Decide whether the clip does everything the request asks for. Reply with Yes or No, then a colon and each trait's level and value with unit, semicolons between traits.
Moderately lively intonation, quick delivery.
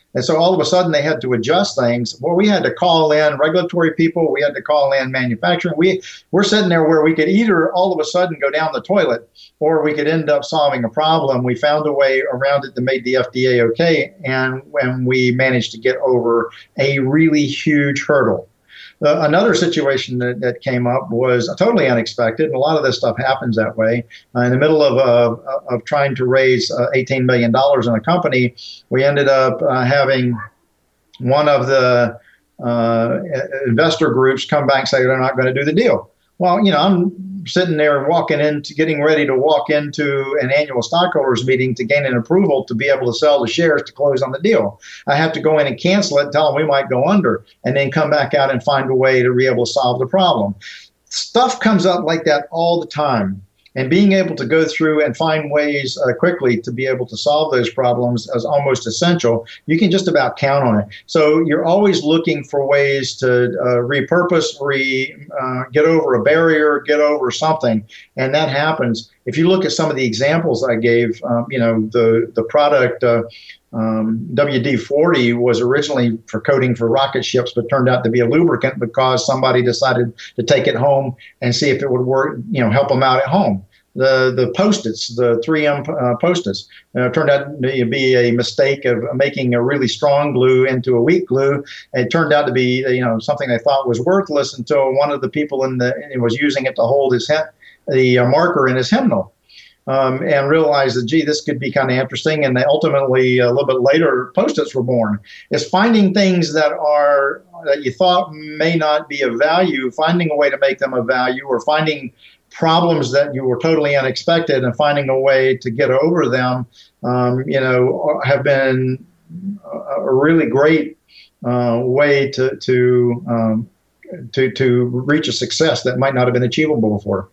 Yes: average, 3.8 semitones; fast, 210 wpm